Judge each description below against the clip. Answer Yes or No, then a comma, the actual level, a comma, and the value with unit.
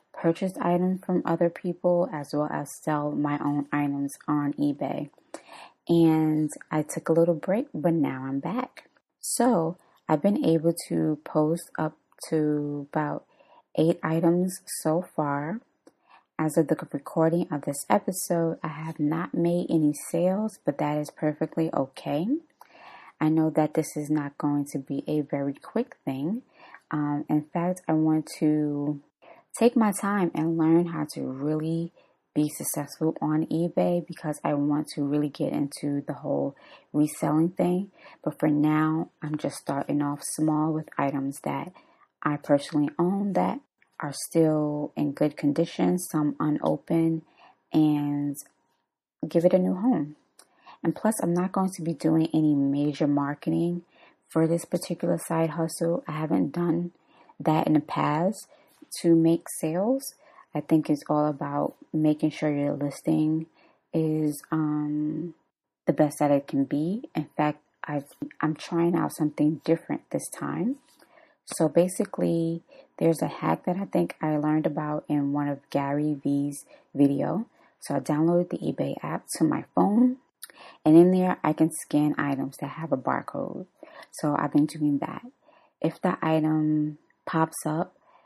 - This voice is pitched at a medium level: Yes, medium, 155 Hz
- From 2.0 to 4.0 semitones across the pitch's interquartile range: Yes, narrow, 2.6 semitones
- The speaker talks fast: No, average, 155 wpm